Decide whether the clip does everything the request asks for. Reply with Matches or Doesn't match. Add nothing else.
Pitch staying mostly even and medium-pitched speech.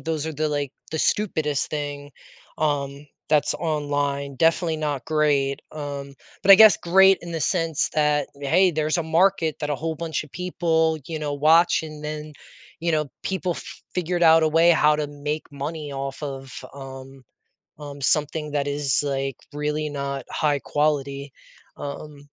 Matches